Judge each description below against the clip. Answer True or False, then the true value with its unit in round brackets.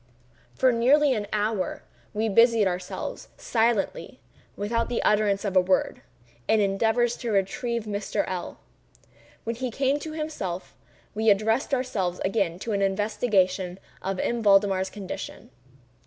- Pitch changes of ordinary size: True (3.4 semitones)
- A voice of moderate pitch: False (210 Hz)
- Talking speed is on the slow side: True (125 wpm)